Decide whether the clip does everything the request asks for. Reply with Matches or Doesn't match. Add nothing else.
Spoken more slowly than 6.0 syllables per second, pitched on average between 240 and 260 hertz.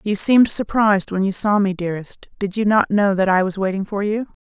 Doesn't match